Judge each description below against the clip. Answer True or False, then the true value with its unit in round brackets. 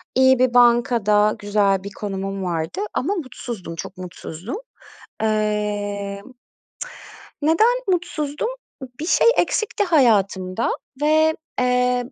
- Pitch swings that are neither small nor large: False (5.8 semitones)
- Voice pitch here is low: False (225 Hz)